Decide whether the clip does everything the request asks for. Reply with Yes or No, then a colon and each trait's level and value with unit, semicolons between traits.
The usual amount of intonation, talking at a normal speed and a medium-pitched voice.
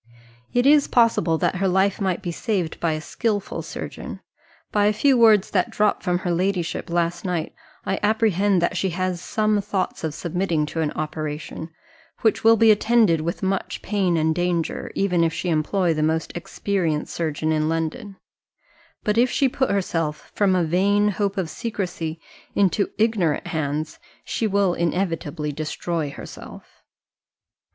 Yes: average, 4.0 semitones; average, 160 wpm; medium, 180 Hz